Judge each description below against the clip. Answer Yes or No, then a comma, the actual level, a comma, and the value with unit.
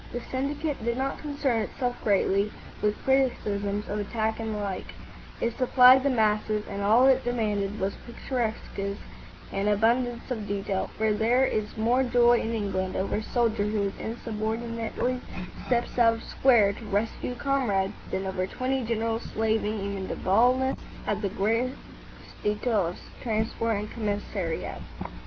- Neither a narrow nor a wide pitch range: Yes, average, 3.0 semitones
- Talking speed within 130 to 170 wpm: Yes, average, 150 wpm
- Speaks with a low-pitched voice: No, high, 220 Hz